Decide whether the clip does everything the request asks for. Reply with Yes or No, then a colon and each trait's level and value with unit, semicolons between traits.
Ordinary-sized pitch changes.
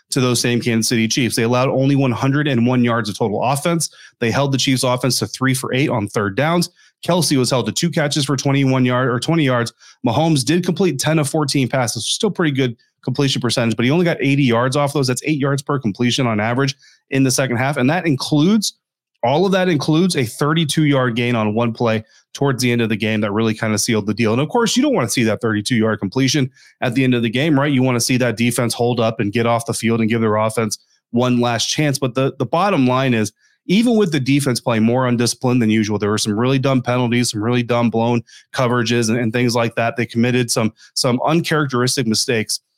Yes: average, 3.3 semitones